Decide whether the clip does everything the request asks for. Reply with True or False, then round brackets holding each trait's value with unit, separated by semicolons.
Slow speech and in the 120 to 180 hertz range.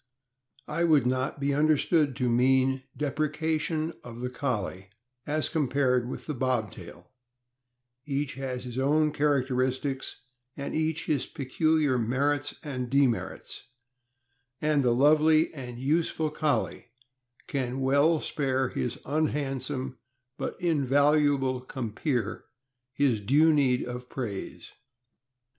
True (115 wpm; 135 Hz)